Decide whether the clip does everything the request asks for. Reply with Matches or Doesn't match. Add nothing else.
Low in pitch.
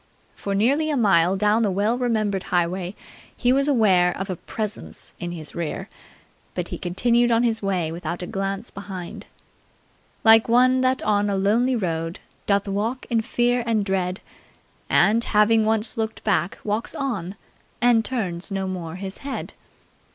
Doesn't match